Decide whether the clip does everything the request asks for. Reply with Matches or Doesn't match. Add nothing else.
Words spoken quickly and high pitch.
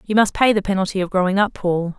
Matches